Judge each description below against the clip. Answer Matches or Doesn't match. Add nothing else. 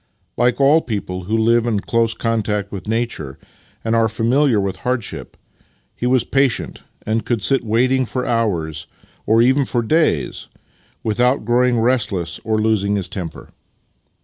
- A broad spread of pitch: Doesn't match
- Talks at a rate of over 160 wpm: Doesn't match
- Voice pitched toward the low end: Matches